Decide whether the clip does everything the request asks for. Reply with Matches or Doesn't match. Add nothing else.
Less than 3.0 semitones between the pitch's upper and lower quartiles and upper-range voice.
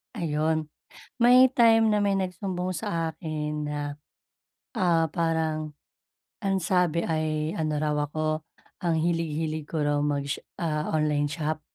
Doesn't match